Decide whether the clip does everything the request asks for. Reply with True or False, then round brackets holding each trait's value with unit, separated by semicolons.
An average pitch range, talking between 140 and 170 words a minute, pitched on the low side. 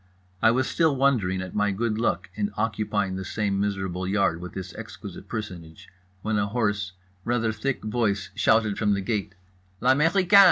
True (3.4 semitones; 165 wpm; 105 Hz)